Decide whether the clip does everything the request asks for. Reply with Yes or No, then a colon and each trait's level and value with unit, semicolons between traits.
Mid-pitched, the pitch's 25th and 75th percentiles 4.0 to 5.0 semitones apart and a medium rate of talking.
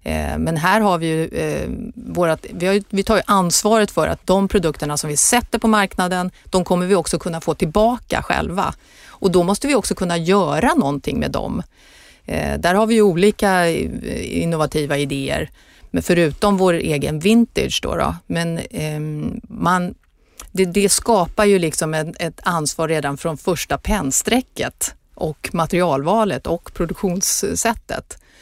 Yes: medium, 180 Hz; average, 4.5 semitones; average, 155 wpm